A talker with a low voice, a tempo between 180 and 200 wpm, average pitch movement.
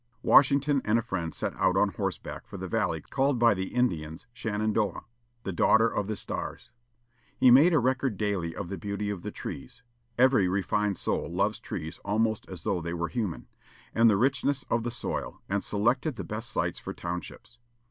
Yes: low, 110 Hz; average, 190 wpm; average, 4.2 semitones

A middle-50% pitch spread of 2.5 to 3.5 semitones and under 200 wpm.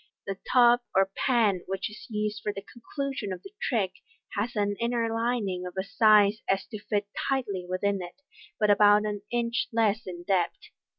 Yes: average, 3.1 semitones; average, 185 wpm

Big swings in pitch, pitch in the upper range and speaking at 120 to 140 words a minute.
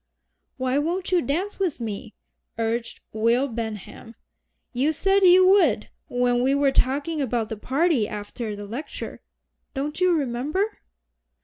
Yes: wide, 6.3 semitones; very high, 265 Hz; slow, 135 wpm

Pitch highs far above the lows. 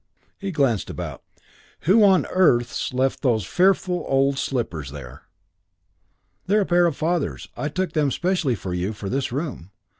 Yes: wide, 7.2 semitones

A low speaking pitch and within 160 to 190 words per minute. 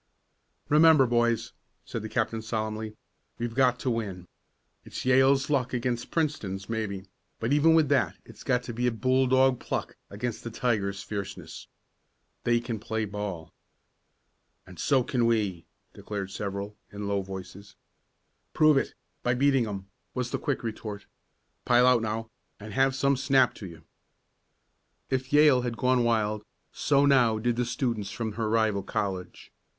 No: low, 115 Hz; average, 150 wpm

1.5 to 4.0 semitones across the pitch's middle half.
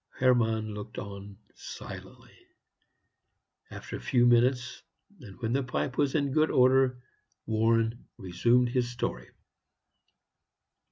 Yes: narrow, 2.5 semitones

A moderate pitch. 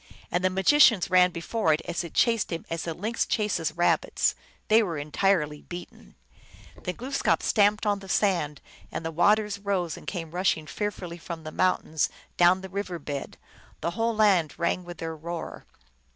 Yes: medium, 180 Hz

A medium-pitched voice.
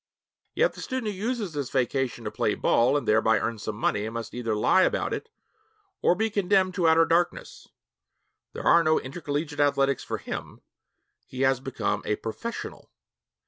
Yes: medium, 145 Hz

